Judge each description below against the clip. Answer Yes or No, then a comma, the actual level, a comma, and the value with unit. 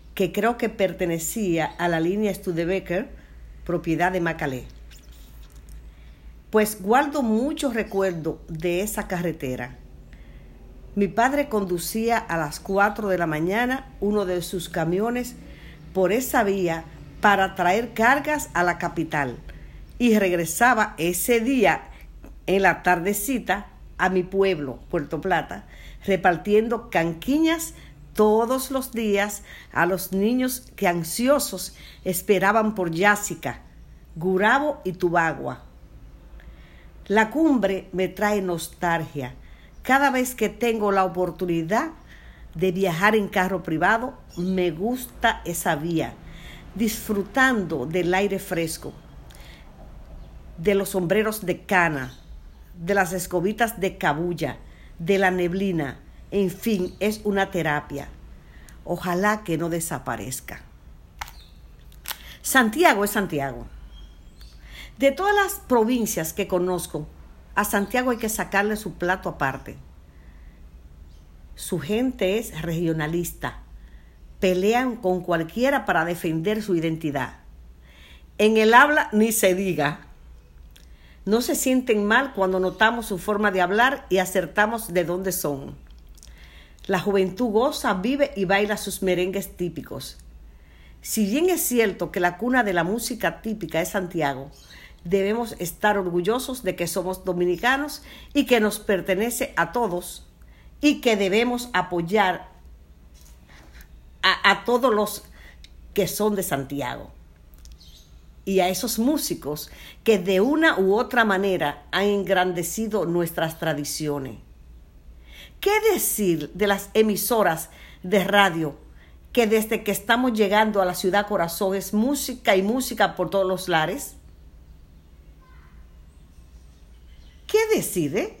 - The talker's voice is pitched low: No, medium, 185 Hz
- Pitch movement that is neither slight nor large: No, wide, 6.5 semitones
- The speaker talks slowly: Yes, slow, 115 wpm